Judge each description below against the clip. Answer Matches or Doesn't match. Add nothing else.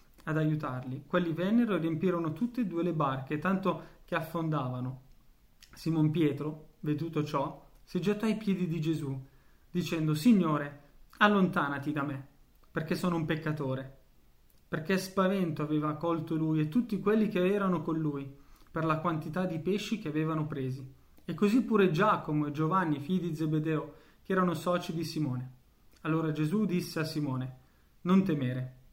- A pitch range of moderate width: Matches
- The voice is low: Doesn't match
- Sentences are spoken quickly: Doesn't match